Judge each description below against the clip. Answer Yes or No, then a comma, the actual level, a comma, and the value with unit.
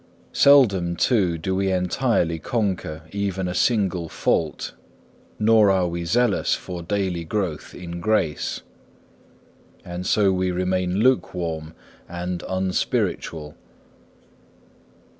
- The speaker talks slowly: Yes, slow, 105 wpm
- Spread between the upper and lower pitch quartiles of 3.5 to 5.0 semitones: No, average, 2.8 semitones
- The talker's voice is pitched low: Yes, very low, 90 Hz